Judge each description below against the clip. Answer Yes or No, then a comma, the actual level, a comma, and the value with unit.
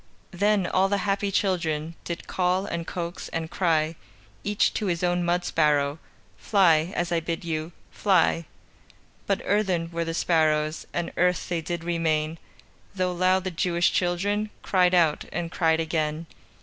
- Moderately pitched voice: Yes, medium, 175 Hz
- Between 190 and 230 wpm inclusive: No, average, 155 wpm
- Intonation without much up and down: Yes, narrow, 2.1 semitones